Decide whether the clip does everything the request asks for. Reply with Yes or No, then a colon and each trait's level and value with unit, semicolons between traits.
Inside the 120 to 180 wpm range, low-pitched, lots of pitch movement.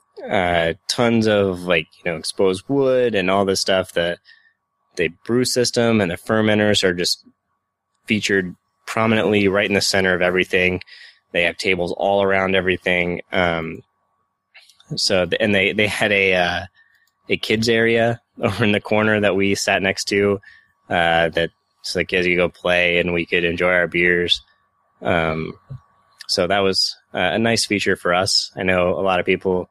No: average, 175 wpm; very low, 95 Hz; average, 3.2 semitones